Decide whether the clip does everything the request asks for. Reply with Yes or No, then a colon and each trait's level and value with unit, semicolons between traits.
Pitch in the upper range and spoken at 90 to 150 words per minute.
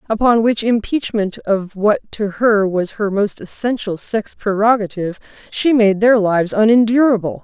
Yes: high, 210 Hz; average, 145 wpm